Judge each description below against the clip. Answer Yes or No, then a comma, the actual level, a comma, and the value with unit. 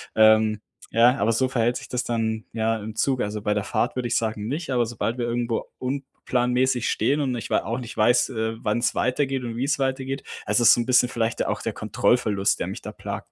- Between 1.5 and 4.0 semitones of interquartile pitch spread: Yes, narrow, 2.4 semitones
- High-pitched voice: No, low, 120 Hz